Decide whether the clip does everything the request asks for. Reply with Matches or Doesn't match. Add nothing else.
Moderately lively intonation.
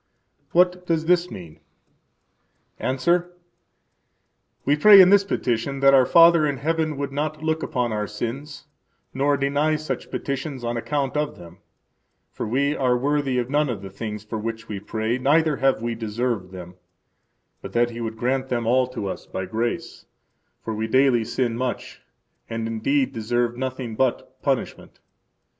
Matches